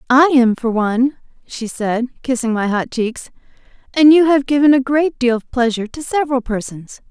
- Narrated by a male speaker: No, female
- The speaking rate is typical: Yes, average, 185 wpm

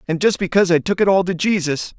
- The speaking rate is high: Yes, fast, 270 wpm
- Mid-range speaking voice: Yes, medium, 180 Hz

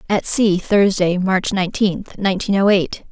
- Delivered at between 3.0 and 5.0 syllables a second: Yes, 4.5 syllables/s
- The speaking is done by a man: No, female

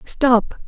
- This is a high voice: Yes, high, 245 Hz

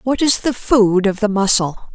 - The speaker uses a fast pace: Yes, fast, 215 wpm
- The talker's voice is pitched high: Yes, high, 215 Hz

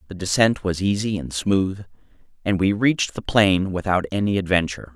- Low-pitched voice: Yes, very low, 95 Hz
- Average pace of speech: Yes, average, 170 wpm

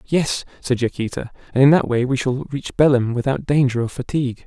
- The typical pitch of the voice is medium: No, low, 130 Hz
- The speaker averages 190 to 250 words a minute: Yes, average, 200 wpm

